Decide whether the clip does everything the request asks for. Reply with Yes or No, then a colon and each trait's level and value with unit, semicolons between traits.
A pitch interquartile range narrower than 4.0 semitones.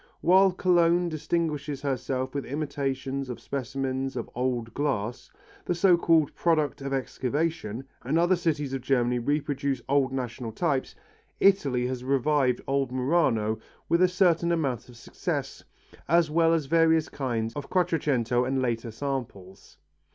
No: average, 4.4 semitones